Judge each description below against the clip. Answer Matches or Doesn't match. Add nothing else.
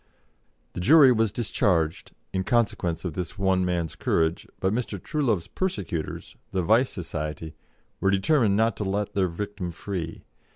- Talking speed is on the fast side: Doesn't match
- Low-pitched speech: Matches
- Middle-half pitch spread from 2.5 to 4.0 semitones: Doesn't match